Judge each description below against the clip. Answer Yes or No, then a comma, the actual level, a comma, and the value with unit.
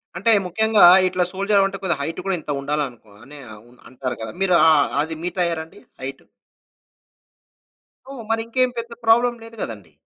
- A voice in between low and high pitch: Yes, medium, 180 Hz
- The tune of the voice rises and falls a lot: Yes, wide, 7.8 semitones